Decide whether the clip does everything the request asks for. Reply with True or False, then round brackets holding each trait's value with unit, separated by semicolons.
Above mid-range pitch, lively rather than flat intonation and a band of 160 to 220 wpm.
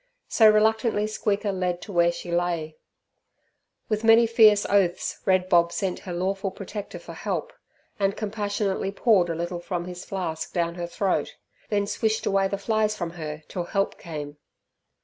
False (195 Hz; 3.4 semitones; 165 wpm)